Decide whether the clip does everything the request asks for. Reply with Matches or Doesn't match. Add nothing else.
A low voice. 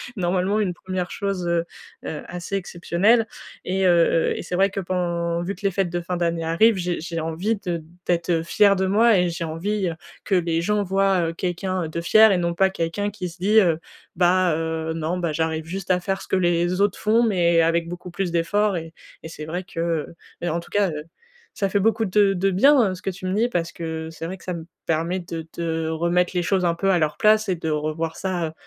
Doesn't match